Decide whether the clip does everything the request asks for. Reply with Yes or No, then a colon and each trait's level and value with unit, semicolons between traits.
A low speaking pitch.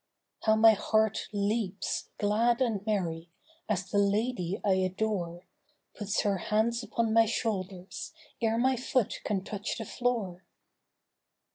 No: high, 210 Hz